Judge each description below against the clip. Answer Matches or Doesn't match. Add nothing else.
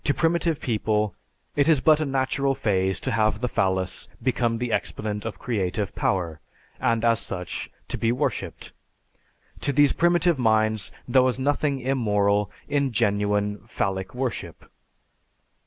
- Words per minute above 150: Doesn't match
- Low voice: Matches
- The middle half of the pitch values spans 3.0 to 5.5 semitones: Matches